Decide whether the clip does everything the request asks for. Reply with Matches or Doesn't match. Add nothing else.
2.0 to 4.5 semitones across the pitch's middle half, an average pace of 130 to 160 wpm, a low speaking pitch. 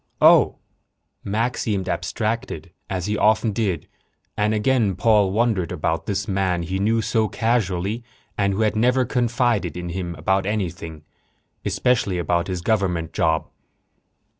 Matches